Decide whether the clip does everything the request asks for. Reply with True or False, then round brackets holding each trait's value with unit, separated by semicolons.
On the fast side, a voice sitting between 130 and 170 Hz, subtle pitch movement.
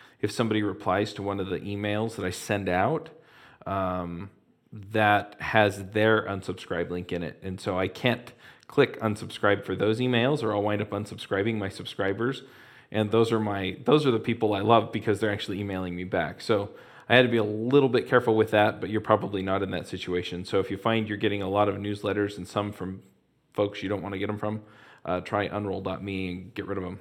False (220 wpm; 105 Hz; 2.1 semitones)